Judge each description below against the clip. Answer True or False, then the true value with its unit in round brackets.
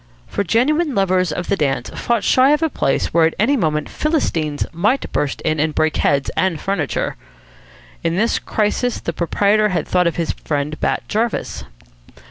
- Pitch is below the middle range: False (185 Hz)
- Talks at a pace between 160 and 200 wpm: True (170 wpm)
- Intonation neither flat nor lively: False (6.4 semitones)